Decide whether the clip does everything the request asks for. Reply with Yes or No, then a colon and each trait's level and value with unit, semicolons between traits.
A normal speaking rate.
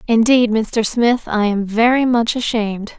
Yes: average, 160 wpm